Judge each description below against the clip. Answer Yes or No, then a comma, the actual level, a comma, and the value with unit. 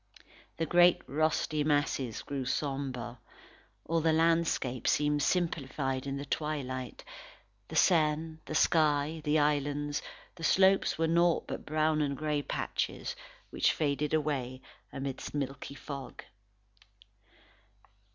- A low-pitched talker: No, medium, 150 Hz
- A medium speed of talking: No, slow, 115 wpm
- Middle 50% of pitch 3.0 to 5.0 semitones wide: No, narrow, 2.4 semitones